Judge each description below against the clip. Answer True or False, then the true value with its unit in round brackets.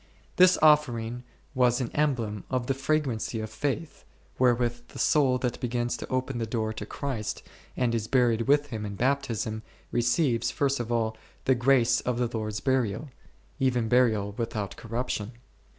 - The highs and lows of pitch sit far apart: False (2.8 semitones)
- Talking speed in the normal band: True (160 wpm)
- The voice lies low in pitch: True (120 Hz)